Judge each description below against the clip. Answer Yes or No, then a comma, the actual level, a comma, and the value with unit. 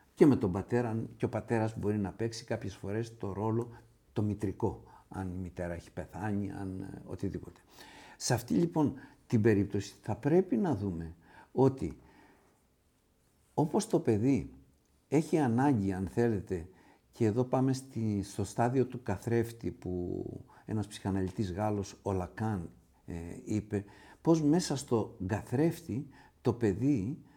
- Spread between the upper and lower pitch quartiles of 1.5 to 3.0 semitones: No, average, 4.4 semitones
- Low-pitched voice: Yes, low, 110 Hz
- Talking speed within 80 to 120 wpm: No, average, 135 wpm